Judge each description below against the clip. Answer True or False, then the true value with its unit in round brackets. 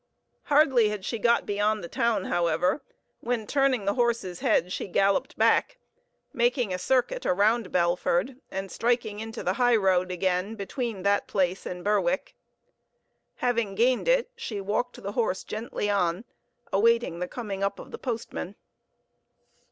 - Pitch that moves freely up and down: False (4.2 semitones)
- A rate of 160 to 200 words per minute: False (150 wpm)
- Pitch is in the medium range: False (210 Hz)